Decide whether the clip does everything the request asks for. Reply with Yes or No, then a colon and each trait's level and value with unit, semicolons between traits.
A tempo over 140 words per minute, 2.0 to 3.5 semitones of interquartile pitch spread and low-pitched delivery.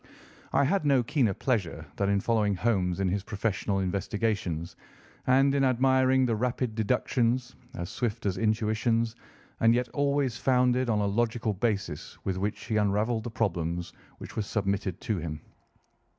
No: average, 155 wpm; average, 4.0 semitones; low, 110 Hz